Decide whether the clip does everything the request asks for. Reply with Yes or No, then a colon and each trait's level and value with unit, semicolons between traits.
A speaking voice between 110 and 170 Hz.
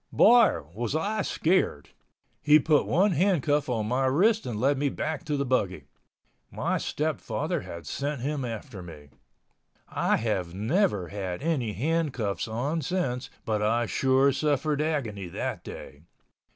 Yes: low, 135 Hz